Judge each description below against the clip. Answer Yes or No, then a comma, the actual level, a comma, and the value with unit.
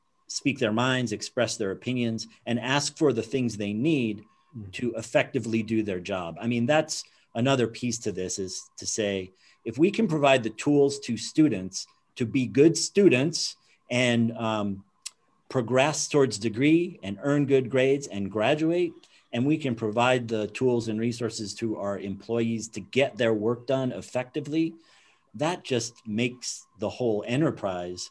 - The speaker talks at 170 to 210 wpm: No, average, 160 wpm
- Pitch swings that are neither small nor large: Yes, average, 4.1 semitones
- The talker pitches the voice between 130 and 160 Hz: No, low, 120 Hz